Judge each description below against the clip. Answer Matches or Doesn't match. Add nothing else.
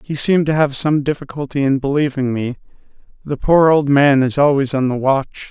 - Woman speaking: Doesn't match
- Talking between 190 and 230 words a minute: Matches